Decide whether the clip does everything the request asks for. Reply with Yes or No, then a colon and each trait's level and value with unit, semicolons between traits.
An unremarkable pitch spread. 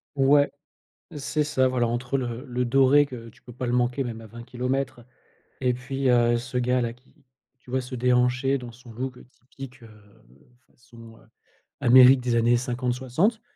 No: narrow, 1.6 semitones